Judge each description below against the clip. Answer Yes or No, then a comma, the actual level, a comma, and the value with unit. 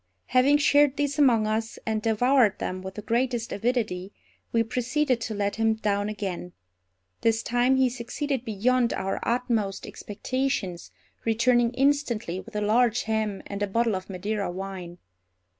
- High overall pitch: Yes, high, 225 Hz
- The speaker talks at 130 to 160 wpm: Yes, average, 150 wpm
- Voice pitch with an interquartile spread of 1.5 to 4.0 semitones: Yes, average, 3.6 semitones